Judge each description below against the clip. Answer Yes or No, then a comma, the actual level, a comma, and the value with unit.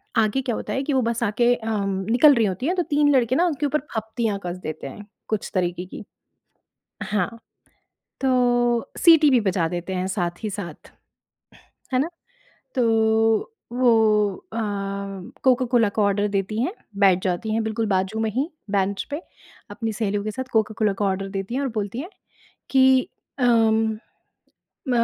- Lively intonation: No, average, 3.9 semitones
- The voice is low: No, high, 220 Hz